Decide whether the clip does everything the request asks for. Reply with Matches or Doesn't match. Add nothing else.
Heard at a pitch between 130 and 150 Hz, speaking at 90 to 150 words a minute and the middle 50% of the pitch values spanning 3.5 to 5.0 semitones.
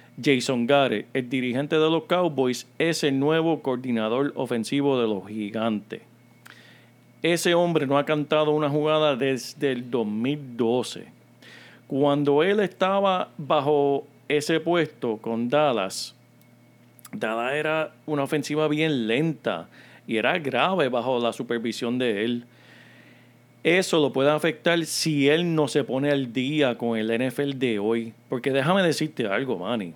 Matches